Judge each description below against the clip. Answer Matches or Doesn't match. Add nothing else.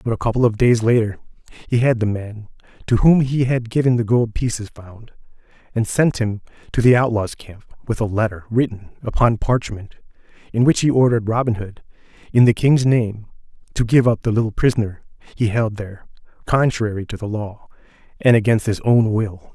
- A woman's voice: Doesn't match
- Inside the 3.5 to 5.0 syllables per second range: Doesn't match